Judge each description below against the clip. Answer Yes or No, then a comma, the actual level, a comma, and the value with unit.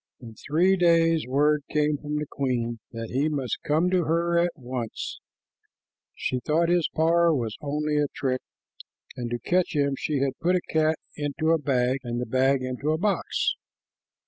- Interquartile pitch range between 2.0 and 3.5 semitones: No, average, 4.3 semitones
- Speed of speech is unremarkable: Yes, average, 175 wpm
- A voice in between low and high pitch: Yes, medium, 150 Hz